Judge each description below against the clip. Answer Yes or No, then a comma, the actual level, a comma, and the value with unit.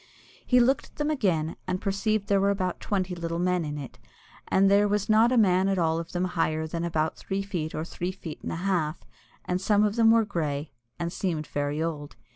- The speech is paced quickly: Yes, fast, 230 wpm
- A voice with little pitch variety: No, average, 3.8 semitones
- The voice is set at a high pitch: No, medium, 180 Hz